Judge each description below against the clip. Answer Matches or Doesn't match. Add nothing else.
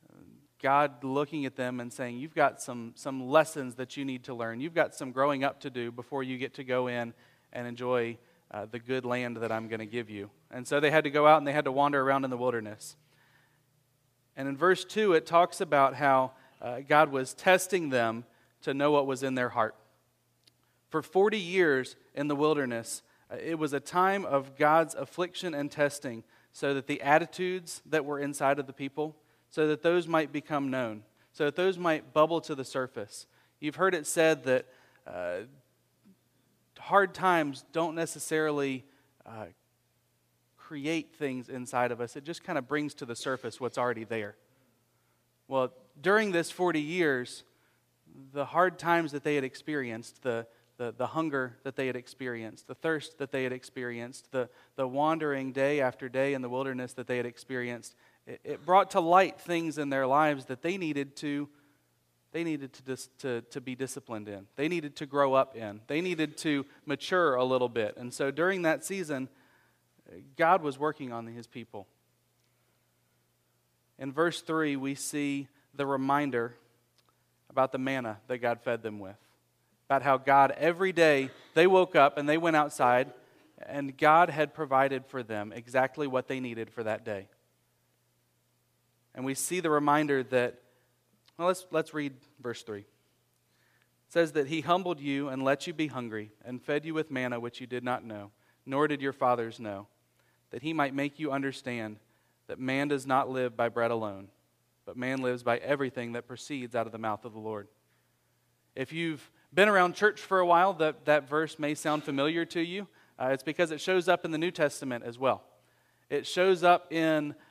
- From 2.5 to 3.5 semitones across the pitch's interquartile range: Doesn't match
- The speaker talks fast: Doesn't match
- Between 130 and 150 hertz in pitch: Matches